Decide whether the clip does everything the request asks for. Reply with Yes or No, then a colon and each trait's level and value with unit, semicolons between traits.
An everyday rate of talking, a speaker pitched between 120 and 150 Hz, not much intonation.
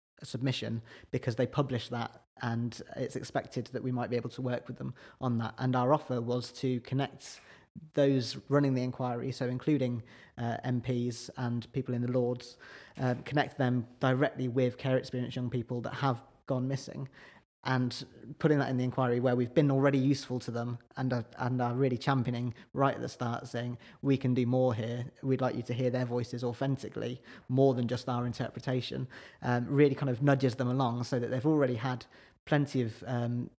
Yes: average, 195 wpm; low, 125 Hz; narrow, 1.6 semitones